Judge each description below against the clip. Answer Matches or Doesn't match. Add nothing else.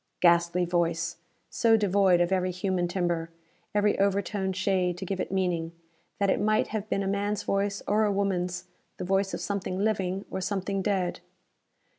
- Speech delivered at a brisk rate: Doesn't match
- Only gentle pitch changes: Matches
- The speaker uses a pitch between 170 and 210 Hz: Matches